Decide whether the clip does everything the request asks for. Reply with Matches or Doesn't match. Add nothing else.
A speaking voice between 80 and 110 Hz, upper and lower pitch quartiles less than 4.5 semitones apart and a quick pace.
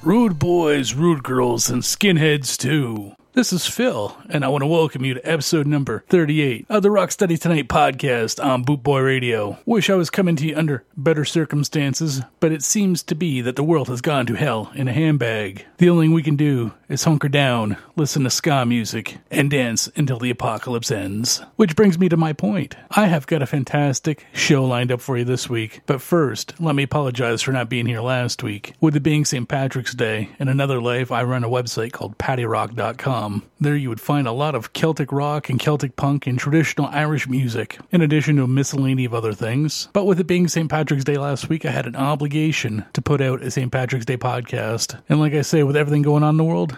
Doesn't match